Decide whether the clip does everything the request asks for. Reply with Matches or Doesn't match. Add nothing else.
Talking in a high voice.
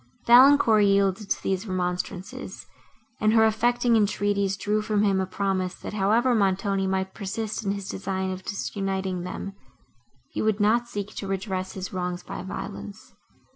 Matches